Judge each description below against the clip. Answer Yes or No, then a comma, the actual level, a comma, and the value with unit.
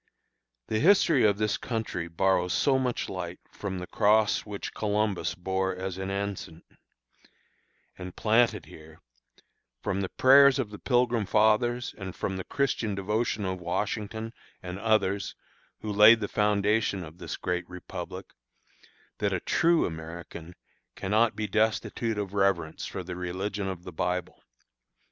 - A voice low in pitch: Yes, low, 100 Hz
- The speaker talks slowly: No, average, 145 wpm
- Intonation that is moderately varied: Yes, average, 3.2 semitones